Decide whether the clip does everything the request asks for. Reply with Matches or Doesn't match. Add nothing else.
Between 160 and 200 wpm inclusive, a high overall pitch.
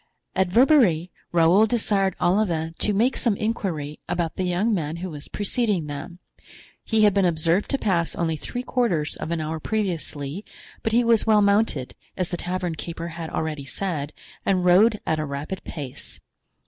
Doesn't match